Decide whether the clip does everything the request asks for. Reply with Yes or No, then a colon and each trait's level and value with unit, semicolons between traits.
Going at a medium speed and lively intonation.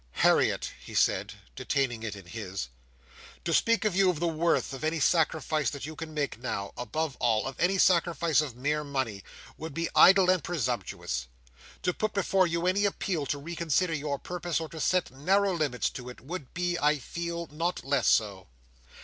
No: average, 180 wpm; average, 4.7 semitones